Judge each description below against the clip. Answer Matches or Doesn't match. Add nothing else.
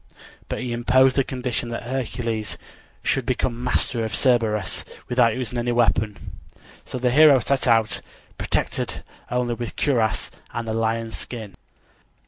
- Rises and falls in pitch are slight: Matches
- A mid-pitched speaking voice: Doesn't match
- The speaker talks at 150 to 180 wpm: Doesn't match